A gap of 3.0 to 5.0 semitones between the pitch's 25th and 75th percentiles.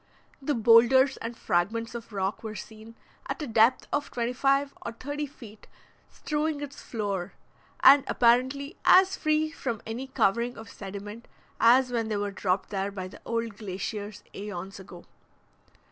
Yes: average, 4.6 semitones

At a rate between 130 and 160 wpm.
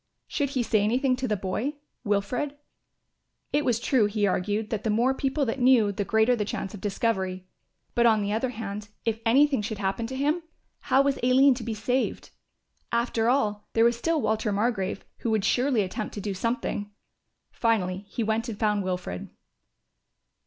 No: average, 180 wpm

